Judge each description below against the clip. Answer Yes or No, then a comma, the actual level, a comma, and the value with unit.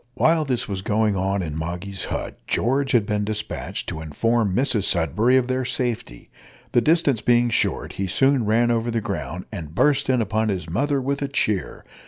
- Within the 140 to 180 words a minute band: No, average, 190 wpm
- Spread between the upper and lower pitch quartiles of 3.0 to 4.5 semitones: No, average, 5.0 semitones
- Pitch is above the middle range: No, low, 110 Hz